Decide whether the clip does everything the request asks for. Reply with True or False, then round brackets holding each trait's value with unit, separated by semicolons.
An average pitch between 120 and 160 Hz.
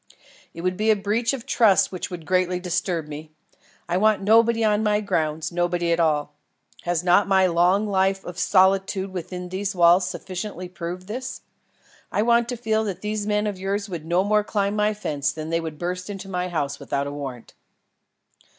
False (185 Hz)